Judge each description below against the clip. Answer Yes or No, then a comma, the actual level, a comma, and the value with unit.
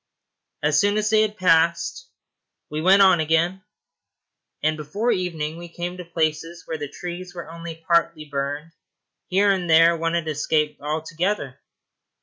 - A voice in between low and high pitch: Yes, medium, 165 Hz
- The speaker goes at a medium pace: Yes, average, 150 wpm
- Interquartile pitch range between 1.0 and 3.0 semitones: Yes, average, 2.7 semitones